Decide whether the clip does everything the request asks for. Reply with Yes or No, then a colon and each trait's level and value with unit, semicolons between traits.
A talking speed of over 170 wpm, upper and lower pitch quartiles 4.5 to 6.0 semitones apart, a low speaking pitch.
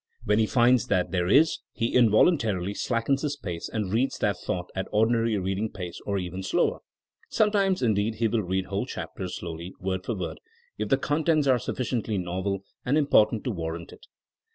Yes: average, 190 wpm; average, 4.9 semitones; low, 110 Hz